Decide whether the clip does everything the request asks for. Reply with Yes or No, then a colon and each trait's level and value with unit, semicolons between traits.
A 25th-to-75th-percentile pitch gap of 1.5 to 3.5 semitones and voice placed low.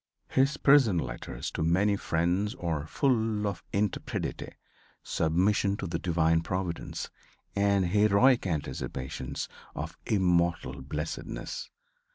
No: average, 4.2 semitones; very low, 95 Hz